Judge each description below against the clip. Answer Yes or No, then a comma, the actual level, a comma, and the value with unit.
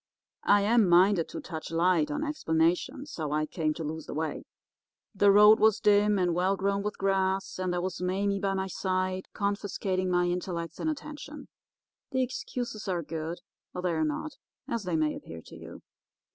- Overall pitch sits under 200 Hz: Yes, medium, 185 Hz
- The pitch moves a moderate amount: Yes, average, 3.3 semitones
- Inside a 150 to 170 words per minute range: No, average, 185 wpm